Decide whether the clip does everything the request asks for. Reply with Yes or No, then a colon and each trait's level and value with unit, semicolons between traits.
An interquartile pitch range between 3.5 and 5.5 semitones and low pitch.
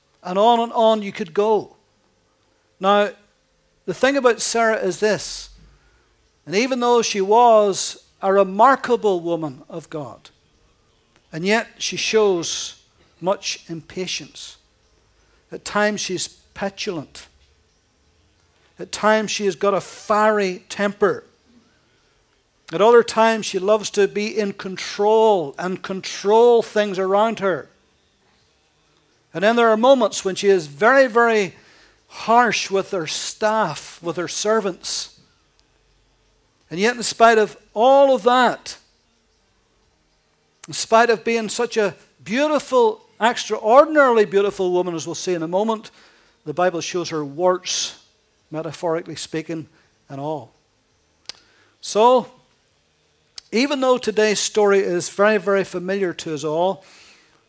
No: average, 4.8 semitones; high, 200 Hz